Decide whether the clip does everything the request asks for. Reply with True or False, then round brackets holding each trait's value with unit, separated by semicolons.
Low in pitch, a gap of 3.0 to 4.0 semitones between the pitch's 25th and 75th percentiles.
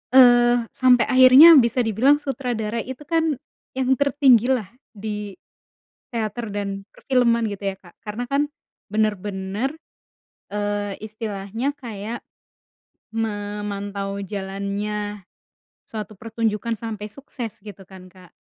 False (215 Hz; 3.4 semitones)